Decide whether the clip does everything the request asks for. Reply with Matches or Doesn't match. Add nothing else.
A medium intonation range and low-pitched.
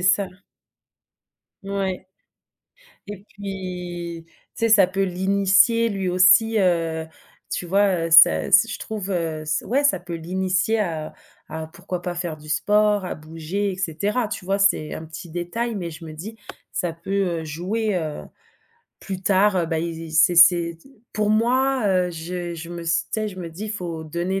Doesn't match